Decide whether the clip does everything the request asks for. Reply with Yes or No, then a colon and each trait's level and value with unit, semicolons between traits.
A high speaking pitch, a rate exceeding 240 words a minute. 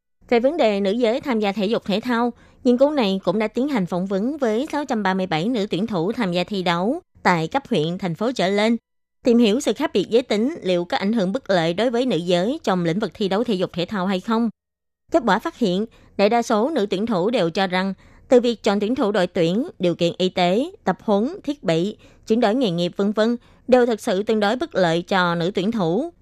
Yes: high, 210 Hz; fast, 250 wpm